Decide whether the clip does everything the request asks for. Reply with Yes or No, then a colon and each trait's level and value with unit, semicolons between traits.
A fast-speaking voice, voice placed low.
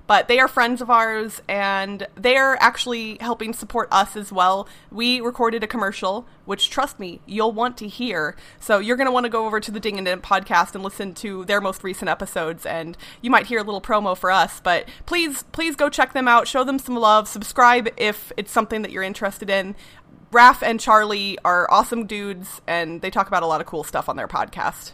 No: fast, 220 wpm; high, 215 Hz